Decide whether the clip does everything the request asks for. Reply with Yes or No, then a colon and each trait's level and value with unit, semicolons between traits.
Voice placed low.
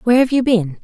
No: high, 225 Hz